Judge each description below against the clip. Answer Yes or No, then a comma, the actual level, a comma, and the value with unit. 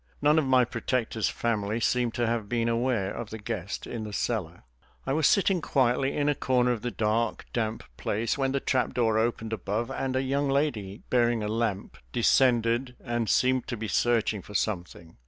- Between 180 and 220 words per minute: Yes, average, 190 wpm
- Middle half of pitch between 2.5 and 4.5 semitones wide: Yes, average, 2.8 semitones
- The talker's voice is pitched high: No, low, 120 Hz